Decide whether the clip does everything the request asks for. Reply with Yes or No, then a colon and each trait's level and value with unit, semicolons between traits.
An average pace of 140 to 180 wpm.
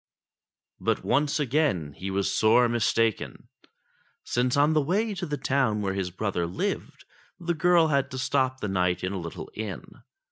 Yes: average, 170 wpm